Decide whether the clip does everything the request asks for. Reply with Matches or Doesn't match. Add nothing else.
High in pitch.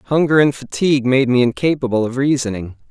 Doesn't match